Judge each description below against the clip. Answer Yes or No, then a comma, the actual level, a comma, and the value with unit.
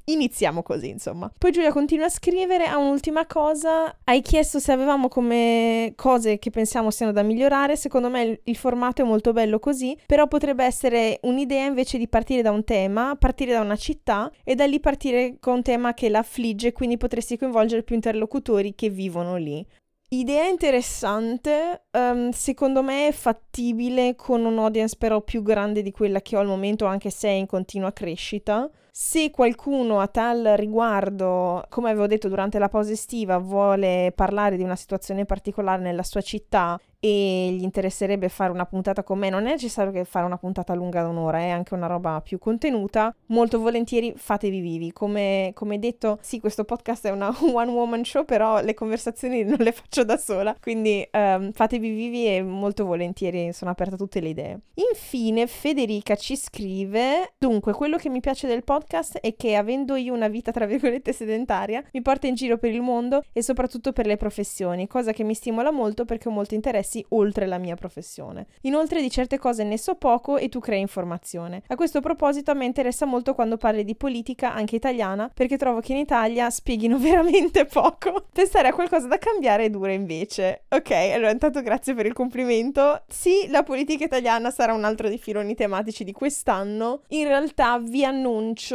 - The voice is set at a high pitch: Yes, high, 230 Hz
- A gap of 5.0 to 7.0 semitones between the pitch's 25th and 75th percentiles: No, average, 4.5 semitones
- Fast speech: Yes, fast, 185 wpm